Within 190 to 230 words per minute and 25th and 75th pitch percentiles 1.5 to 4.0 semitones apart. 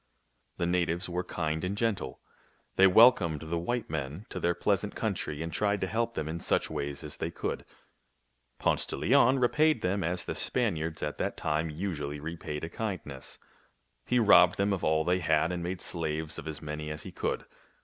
No: average, 200 wpm; average, 4.4 semitones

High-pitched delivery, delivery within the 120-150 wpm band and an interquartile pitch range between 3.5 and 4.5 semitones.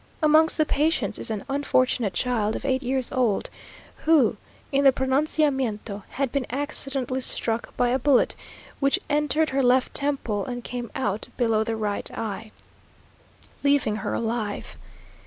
Yes: very high, 255 Hz; average, 145 wpm; average, 3.9 semitones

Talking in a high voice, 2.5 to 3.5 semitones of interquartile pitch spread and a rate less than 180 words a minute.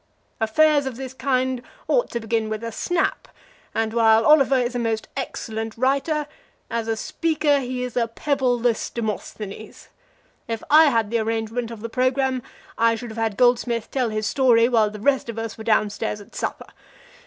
No: high, 235 Hz; average, 2.8 semitones; average, 185 wpm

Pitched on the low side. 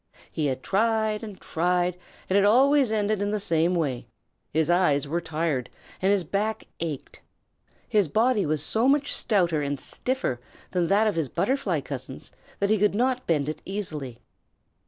No: medium, 185 Hz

